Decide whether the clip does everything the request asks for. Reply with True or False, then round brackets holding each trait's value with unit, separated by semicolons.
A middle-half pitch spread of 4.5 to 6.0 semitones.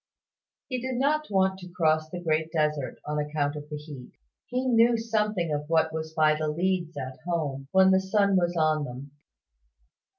False (4.0 semitones)